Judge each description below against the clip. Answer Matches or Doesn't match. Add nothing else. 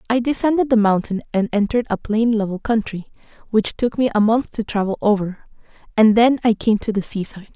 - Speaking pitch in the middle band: Doesn't match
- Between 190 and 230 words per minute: Matches